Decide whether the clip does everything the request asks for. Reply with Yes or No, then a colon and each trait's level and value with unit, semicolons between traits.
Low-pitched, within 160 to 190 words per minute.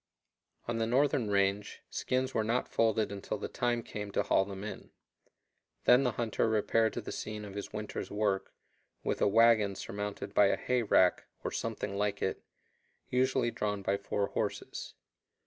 Yes: low, 105 Hz; average, 170 wpm